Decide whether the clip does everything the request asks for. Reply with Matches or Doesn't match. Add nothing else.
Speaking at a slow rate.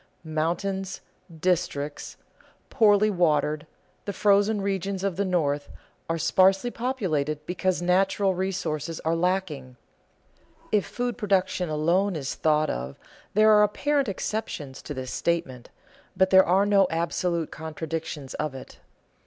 Matches